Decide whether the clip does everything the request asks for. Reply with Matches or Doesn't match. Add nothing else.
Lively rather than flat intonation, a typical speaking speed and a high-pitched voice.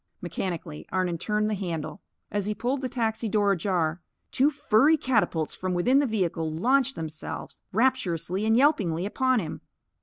Matches